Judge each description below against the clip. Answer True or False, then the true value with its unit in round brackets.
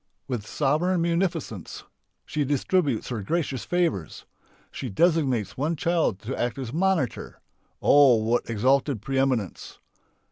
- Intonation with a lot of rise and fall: True (6.0 semitones)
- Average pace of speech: False (120 wpm)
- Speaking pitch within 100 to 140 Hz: True (135 Hz)